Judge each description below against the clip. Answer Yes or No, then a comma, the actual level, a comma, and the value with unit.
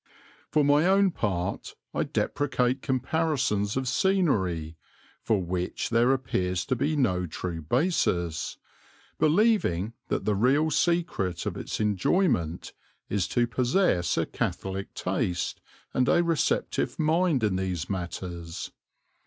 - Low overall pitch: Yes, low, 115 Hz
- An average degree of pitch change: No, wide, 8.9 semitones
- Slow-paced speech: Yes, slow, 120 wpm